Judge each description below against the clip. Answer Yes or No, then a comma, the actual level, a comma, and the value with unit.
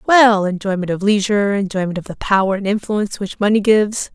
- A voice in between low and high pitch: No, high, 200 Hz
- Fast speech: No, average, 175 wpm